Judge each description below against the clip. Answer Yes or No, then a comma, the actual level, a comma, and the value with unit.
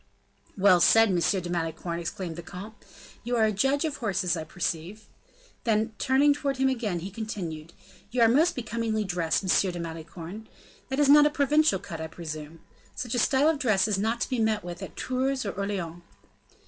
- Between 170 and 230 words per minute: Yes, average, 195 wpm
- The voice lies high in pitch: Yes, high, 205 Hz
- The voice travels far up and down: Yes, wide, 6.5 semitones